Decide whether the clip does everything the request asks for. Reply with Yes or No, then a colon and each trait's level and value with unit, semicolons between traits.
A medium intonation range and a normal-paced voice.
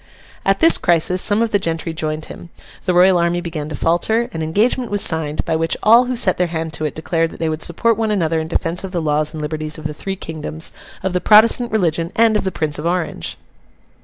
No: average, 3.8 semitones; fast, 240 wpm